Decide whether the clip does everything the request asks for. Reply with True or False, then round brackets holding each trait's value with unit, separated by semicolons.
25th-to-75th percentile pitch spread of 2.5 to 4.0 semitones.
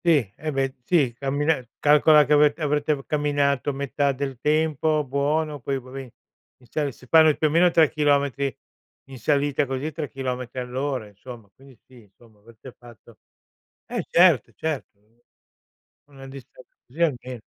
True (2.8 semitones)